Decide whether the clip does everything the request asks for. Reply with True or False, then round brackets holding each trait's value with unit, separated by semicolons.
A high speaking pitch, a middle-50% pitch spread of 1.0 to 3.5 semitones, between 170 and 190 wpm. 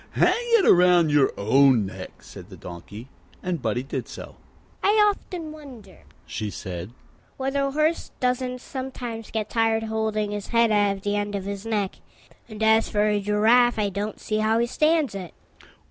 False (215 Hz; 4.5 semitones; 175 wpm)